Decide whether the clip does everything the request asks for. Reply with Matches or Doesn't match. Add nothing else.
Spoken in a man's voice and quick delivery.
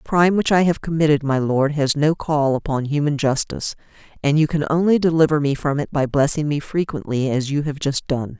Doesn't match